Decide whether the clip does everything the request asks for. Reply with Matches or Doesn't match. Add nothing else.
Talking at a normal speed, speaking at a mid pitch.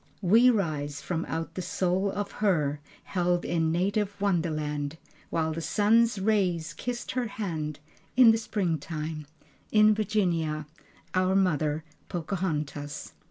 Doesn't match